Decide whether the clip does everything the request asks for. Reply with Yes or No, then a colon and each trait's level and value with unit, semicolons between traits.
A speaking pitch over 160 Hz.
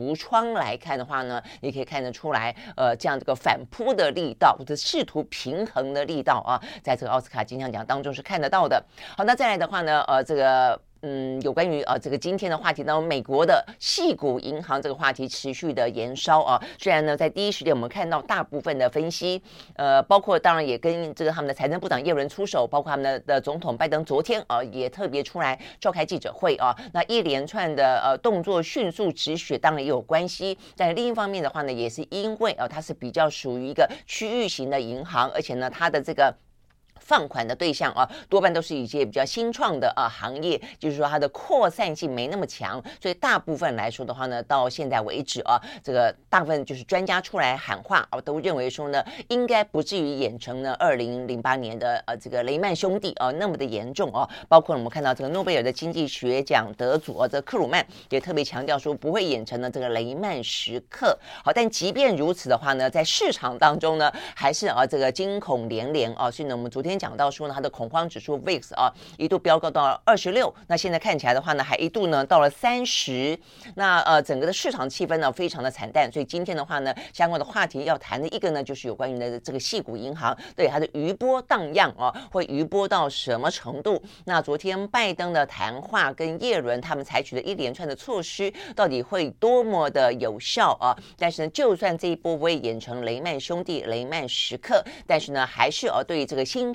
No: medium, 150 Hz